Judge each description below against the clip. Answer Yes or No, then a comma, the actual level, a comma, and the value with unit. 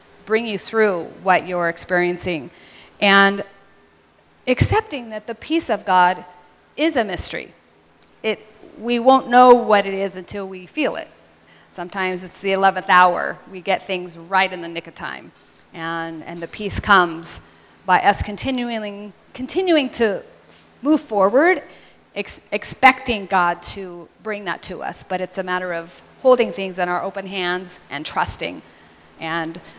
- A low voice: No, high, 190 Hz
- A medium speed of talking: Yes, average, 150 wpm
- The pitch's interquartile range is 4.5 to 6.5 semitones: No, average, 3.8 semitones